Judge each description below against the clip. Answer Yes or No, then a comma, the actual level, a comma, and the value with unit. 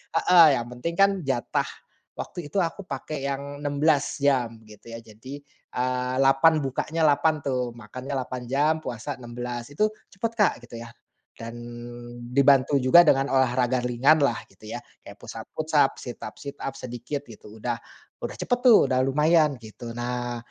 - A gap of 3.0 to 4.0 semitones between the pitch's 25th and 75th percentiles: Yes, average, 3.3 semitones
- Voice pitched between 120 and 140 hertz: Yes, low, 135 Hz